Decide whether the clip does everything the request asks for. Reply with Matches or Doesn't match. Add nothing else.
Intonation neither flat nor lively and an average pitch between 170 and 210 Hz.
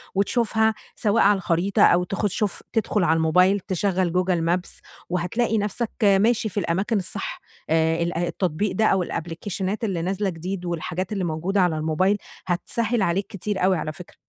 Matches